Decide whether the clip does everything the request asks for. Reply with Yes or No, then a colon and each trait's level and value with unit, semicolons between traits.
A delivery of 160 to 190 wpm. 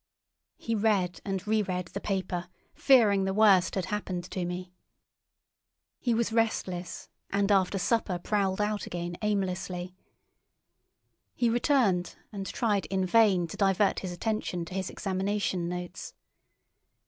No: slow, 135 wpm